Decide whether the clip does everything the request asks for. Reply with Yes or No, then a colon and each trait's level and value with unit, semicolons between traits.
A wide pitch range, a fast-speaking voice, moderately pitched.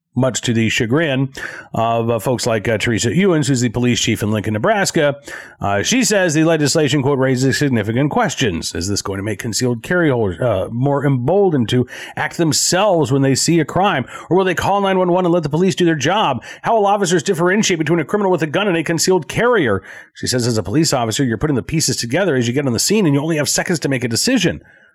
Yes: wide, 6.3 semitones; fast, 235 wpm; medium, 145 Hz